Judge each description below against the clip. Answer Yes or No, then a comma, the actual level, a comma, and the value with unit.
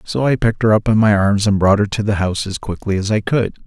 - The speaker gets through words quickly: Yes, fast, 310 wpm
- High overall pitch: No, low, 105 Hz